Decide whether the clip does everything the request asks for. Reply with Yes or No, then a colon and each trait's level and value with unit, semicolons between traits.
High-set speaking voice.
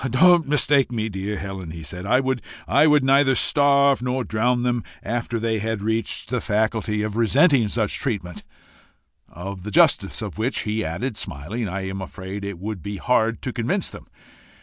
No: low, 110 Hz